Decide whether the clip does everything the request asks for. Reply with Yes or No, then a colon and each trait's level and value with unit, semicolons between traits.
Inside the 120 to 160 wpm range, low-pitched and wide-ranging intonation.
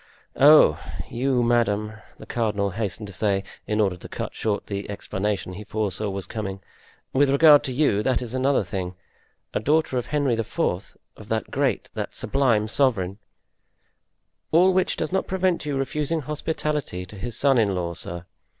No: average, 170 wpm; low, 115 Hz; wide, 5.8 semitones